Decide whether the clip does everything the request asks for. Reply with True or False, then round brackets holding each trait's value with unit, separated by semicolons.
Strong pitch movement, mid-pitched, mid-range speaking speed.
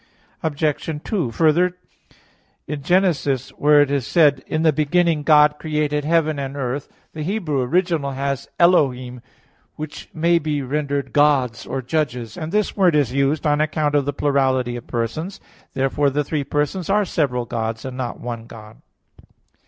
False (3.0 semitones; 145 Hz; 160 wpm)